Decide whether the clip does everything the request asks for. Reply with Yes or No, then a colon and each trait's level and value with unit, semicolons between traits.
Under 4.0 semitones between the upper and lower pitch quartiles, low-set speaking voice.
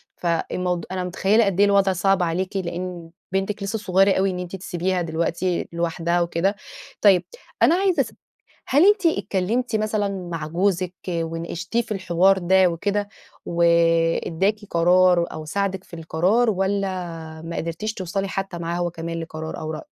No: average, 2.8 semitones; medium, 185 Hz